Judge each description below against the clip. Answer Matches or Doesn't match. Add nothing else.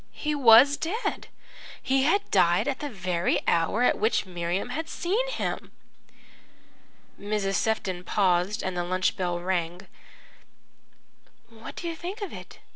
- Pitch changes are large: Matches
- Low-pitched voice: Doesn't match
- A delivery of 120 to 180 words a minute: Matches